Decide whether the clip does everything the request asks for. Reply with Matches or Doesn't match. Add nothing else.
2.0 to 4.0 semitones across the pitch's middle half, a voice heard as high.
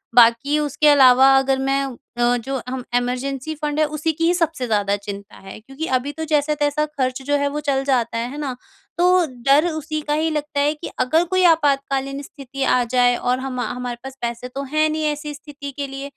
Matches